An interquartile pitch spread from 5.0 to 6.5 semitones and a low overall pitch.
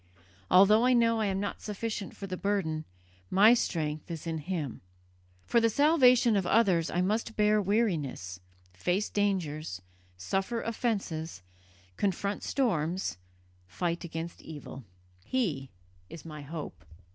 No: average, 5.3 semitones; high, 190 Hz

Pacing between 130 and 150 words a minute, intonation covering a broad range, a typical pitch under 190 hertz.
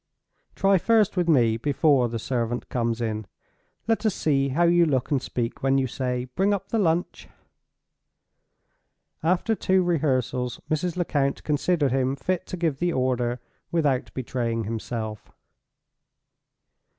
Yes: average, 140 wpm; wide, 5.8 semitones; low, 135 Hz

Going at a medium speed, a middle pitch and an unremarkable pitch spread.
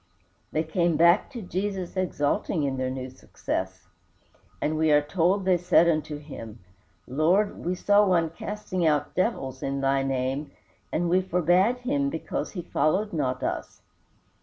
Yes: average, 155 wpm; medium, 170 Hz; average, 4.7 semitones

